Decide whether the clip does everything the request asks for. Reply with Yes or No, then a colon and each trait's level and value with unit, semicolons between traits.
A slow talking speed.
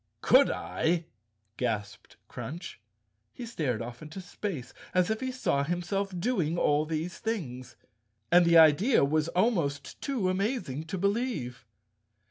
Yes: slow, 130 wpm